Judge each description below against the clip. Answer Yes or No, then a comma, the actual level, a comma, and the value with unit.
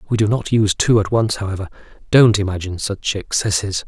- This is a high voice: No, low, 105 Hz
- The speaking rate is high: No, average, 185 wpm